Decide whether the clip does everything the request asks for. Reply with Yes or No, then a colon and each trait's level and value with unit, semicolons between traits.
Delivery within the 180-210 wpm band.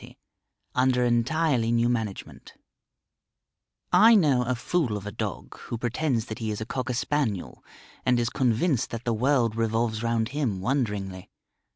No: average, 155 wpm